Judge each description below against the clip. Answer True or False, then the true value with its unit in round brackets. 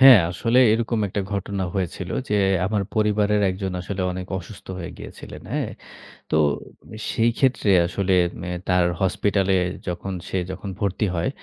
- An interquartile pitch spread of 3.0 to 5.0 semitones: False (2.4 semitones)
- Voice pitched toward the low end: True (100 Hz)